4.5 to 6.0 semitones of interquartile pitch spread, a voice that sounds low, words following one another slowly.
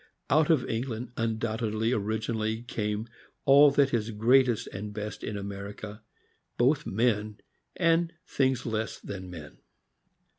No: average, 3.3 semitones; low, 110 Hz; slow, 125 wpm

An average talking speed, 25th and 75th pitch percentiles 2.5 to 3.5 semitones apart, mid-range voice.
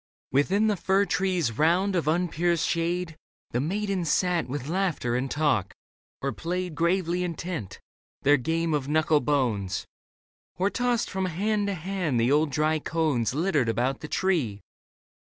No: average, 150 wpm; average, 4.3 semitones; medium, 165 Hz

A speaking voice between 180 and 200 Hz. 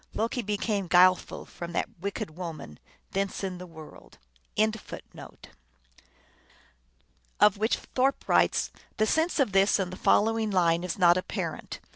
Yes: medium, 185 Hz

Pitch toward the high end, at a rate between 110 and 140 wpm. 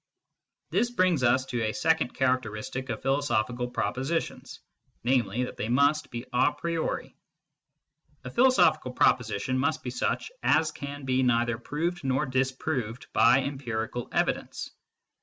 No: low, 130 Hz; slow, 135 wpm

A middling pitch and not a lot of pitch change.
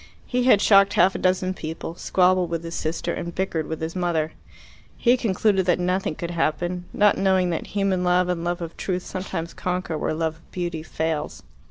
Yes: medium, 180 Hz; narrow, 2.2 semitones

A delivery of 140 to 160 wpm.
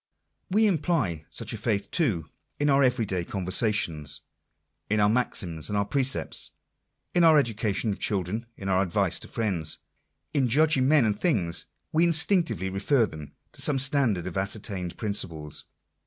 Yes: average, 155 wpm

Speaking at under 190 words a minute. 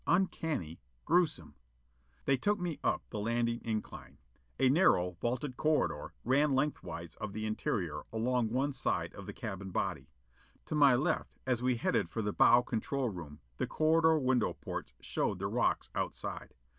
Yes: average, 160 wpm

